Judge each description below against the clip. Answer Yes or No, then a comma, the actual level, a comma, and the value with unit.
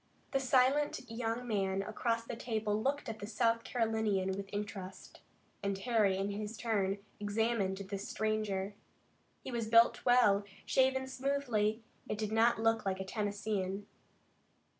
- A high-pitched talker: Yes, high, 220 Hz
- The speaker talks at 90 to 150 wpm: Yes, average, 140 wpm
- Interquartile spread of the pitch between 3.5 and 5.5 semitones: No, average, 2.8 semitones